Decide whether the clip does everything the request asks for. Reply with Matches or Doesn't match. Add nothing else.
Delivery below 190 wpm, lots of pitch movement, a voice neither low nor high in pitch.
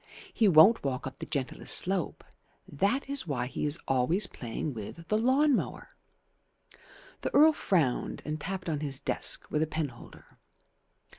Matches